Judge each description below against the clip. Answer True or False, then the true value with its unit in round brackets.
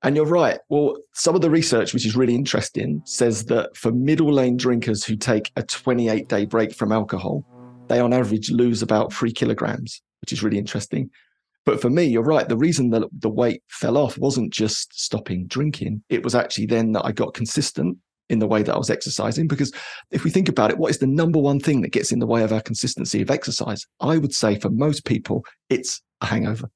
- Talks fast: True (220 wpm)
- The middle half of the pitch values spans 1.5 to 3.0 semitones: False (4.3 semitones)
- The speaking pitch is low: True (120 Hz)